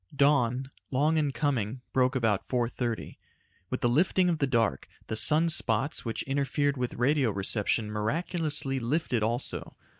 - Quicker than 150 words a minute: No, average, 145 wpm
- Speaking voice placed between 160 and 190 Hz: No, low, 130 Hz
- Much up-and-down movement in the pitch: No, average, 3.9 semitones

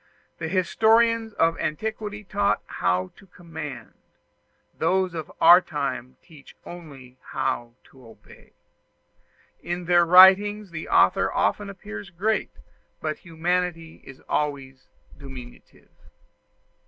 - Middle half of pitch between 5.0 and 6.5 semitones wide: Yes, average, 5.3 semitones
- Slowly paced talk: Yes, slow, 105 wpm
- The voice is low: No, medium, 170 Hz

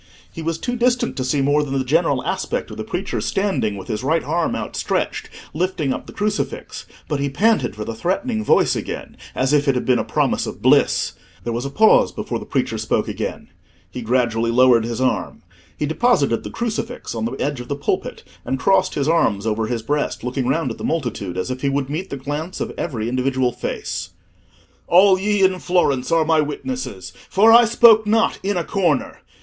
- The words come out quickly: Yes, fast, 210 wpm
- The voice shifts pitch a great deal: Yes, wide, 6.9 semitones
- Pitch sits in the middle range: Yes, medium, 145 Hz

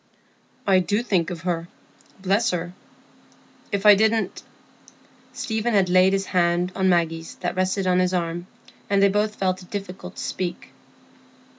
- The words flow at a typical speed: Yes, average, 150 wpm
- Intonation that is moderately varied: No, narrow, 2.0 semitones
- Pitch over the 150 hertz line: Yes, medium, 185 Hz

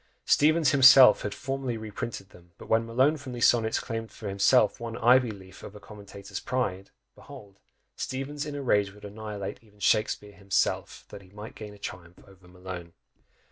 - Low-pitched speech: Yes, low, 105 Hz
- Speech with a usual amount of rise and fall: Yes, average, 4.2 semitones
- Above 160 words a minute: Yes, average, 180 wpm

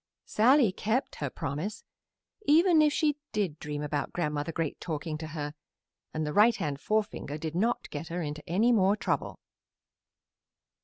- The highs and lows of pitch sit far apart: Yes, wide, 6.6 semitones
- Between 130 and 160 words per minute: Yes, average, 155 wpm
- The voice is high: No, medium, 170 Hz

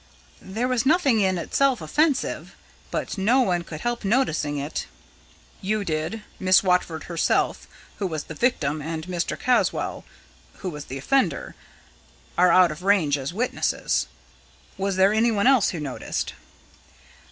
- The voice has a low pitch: No, high, 190 Hz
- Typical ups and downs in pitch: No, wide, 6.6 semitones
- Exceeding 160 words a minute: No, average, 140 wpm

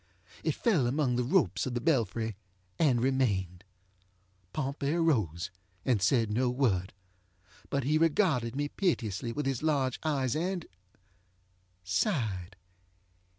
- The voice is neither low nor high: No, low, 125 Hz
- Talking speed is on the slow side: Yes, slow, 115 wpm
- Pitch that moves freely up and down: Yes, wide, 7.1 semitones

